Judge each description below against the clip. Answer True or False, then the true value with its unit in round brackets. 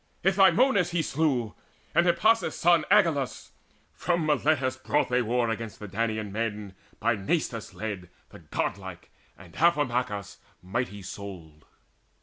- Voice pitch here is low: True (120 Hz)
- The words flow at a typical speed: False (130 wpm)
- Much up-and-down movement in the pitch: True (7.8 semitones)